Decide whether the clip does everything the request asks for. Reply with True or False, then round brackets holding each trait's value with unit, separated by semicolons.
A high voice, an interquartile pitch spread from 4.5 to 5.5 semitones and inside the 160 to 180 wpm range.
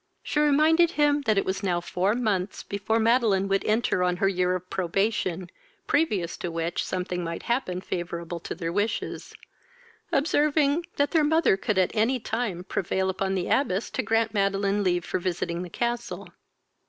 True (195 Hz; 4.8 semitones; 170 wpm)